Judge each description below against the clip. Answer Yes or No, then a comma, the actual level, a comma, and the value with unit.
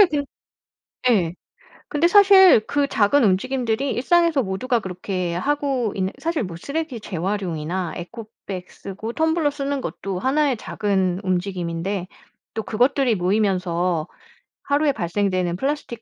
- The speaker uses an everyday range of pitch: No, wide, 7.4 semitones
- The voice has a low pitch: No, high, 215 Hz